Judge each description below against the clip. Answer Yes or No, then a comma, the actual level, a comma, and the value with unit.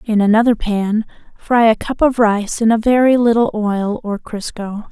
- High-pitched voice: Yes, high, 220 Hz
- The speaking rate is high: No, average, 185 wpm